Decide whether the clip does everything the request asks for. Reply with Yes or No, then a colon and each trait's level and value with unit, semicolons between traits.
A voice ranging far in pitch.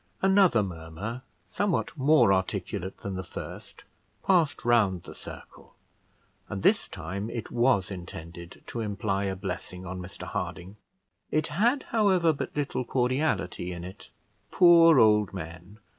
Yes: wide, 8.1 semitones